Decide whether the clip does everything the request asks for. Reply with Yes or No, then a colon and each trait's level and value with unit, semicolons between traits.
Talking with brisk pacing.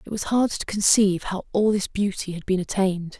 Yes: fast, 225 wpm